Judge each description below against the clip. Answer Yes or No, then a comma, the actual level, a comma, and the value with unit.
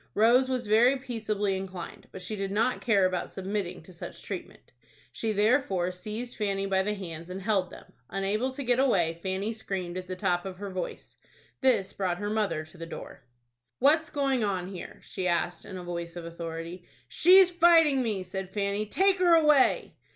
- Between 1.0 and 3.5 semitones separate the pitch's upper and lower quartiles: No, average, 4.9 semitones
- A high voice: Yes, high, 200 Hz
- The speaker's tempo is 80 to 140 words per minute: No, average, 190 wpm